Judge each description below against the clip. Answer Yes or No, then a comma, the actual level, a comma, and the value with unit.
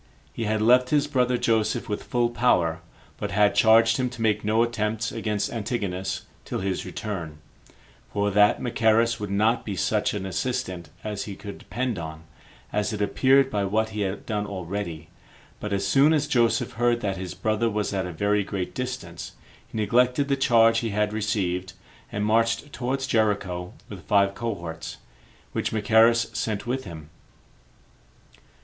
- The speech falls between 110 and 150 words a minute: No, average, 165 wpm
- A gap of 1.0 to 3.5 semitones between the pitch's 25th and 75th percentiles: Yes, average, 3.1 semitones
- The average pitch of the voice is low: Yes, low, 105 Hz